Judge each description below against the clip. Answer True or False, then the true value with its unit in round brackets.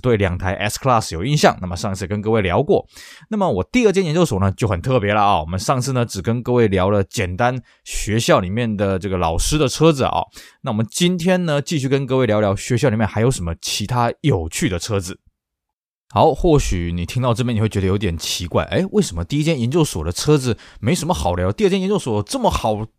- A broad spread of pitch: True (6.5 semitones)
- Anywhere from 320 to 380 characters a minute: True (350 characters per minute)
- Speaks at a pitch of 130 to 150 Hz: False (110 Hz)